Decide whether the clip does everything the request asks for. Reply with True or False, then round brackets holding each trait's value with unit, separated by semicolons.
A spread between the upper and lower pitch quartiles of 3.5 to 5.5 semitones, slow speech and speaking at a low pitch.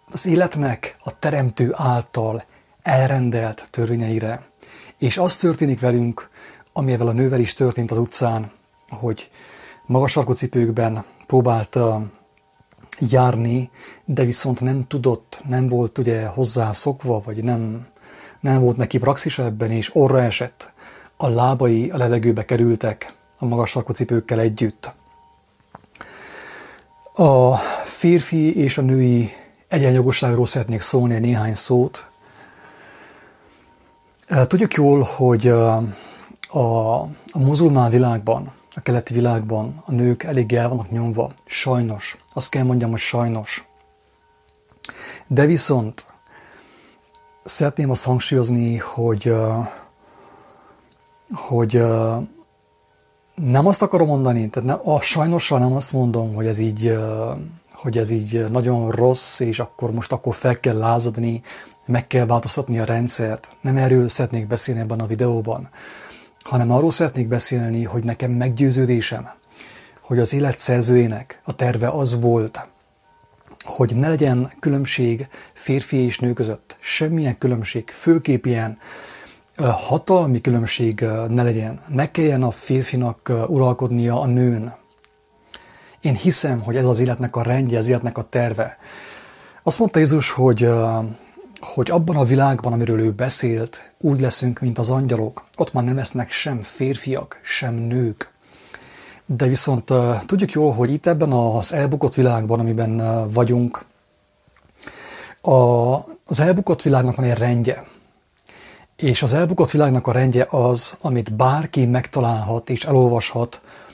False (2.5 semitones; 125 wpm; 125 Hz)